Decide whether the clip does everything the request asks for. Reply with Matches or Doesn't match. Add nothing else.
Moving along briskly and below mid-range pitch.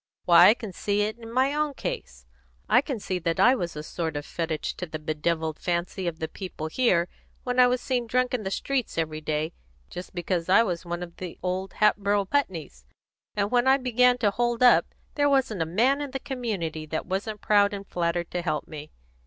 Doesn't match